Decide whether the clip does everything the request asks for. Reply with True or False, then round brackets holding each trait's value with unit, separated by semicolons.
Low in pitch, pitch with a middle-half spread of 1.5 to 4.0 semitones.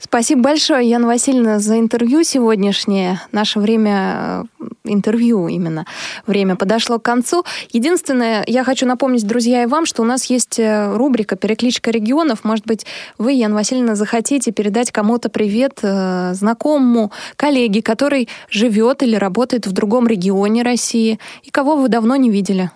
False (235 Hz; 2.9 semitones)